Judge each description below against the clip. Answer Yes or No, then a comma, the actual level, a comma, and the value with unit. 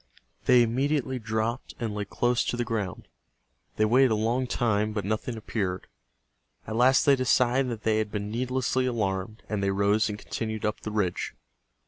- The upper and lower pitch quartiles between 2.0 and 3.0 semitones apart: Yes, average, 2.7 semitones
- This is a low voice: Yes, low, 110 Hz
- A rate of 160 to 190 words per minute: Yes, average, 175 wpm